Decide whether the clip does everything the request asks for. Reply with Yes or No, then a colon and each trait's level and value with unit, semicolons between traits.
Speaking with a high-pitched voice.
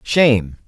No: low, 115 Hz